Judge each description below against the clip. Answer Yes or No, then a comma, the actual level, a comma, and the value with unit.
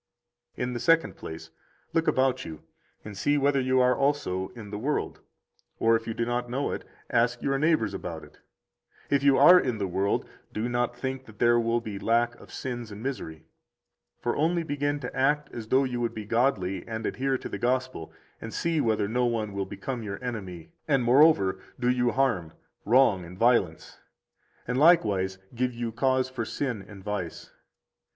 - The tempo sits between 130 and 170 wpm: No, average, 190 wpm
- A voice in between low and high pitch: No, low, 120 Hz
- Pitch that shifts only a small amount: No, average, 4.3 semitones